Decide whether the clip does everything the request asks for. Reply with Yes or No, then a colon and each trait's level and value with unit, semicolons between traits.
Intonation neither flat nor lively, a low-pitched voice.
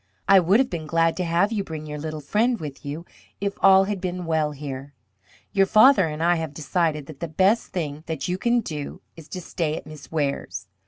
No: average, 4.1 semitones; medium, 165 Hz